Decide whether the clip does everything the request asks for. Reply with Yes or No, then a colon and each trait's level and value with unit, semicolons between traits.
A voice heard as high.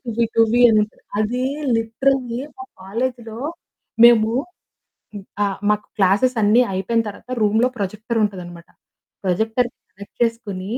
Yes: high, 220 Hz